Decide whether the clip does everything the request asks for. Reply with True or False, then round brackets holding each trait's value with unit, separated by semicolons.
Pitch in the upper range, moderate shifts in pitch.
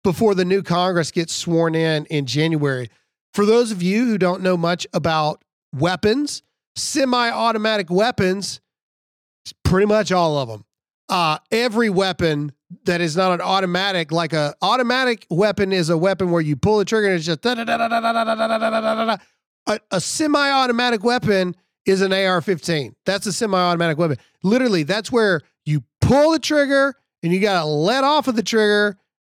True (195 Hz; 4.9 semitones)